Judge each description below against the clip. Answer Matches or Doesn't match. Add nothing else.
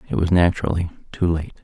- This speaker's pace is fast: Doesn't match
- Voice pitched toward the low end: Matches